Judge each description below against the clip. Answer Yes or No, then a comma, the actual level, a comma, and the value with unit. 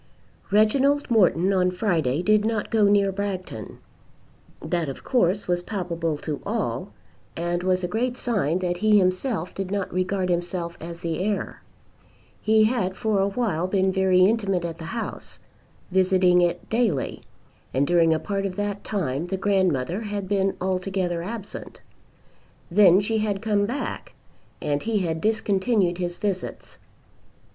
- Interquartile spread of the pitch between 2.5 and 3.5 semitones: Yes, average, 2.9 semitones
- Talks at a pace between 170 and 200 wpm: No, average, 150 wpm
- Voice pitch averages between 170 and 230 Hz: Yes, high, 190 Hz